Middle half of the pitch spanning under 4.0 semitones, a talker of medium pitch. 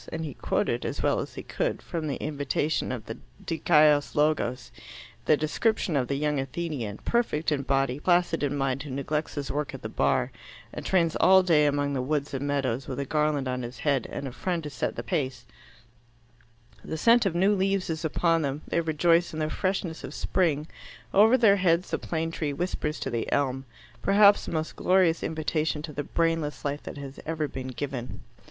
Yes: average, 3.2 semitones; medium, 150 Hz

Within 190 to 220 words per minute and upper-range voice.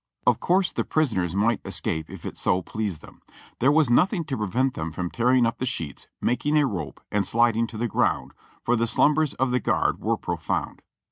No: fast, 205 wpm; low, 115 Hz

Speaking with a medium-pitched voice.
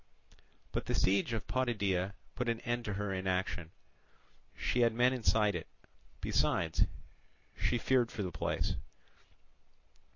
No: low, 105 Hz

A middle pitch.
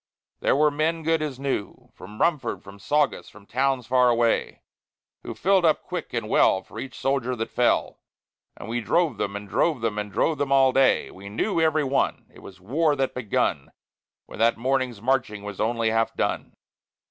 No: low, 130 Hz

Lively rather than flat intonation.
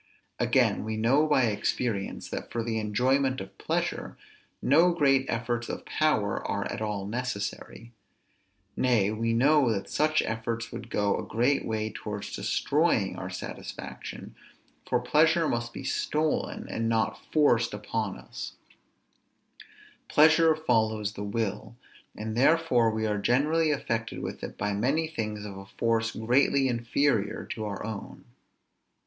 No: average, 4.2 semitones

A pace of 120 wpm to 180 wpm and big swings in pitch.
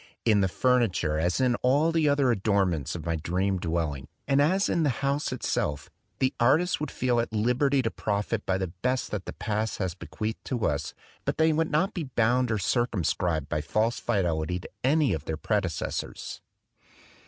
No: average, 190 wpm; wide, 6.8 semitones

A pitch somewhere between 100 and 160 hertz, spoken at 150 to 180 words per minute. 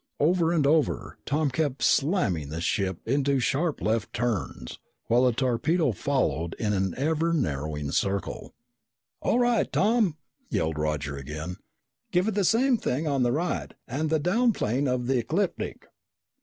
Yes: low, 135 Hz; average, 155 wpm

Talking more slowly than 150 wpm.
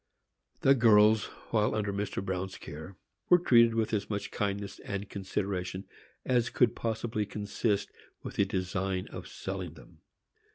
Yes: average, 140 wpm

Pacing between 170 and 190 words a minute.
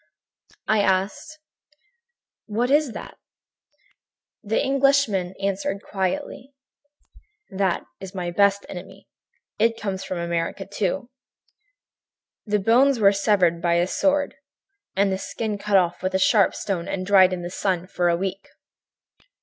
No: slow, 135 wpm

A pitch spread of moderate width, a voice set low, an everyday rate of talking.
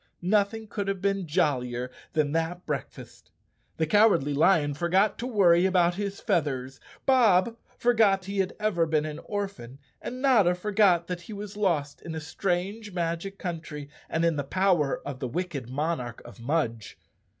No: average, 5.0 semitones; medium, 175 Hz; average, 165 wpm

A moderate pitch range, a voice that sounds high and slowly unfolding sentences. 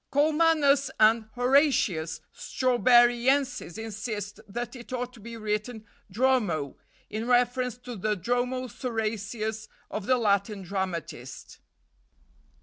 Yes: average, 3.2 semitones; high, 235 Hz; slow, 105 wpm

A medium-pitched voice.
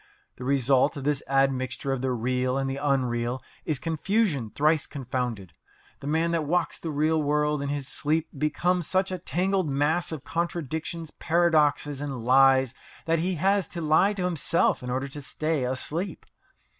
Yes: medium, 145 Hz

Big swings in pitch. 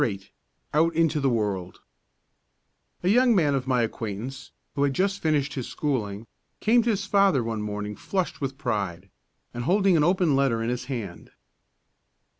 Yes: wide, 7.1 semitones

